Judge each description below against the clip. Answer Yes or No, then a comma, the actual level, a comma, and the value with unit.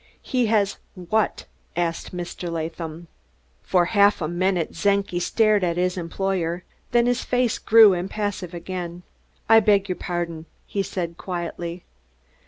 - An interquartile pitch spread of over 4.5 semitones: No, average, 2.9 semitones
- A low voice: No, medium, 180 Hz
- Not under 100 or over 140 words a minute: Yes, slow, 135 wpm